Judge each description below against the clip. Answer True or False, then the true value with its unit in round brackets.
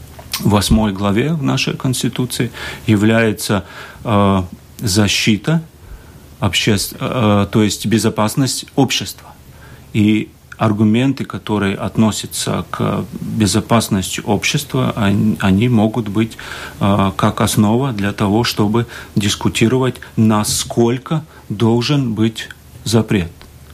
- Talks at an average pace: False (95 wpm)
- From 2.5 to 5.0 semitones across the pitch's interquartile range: True (2.8 semitones)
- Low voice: True (110 Hz)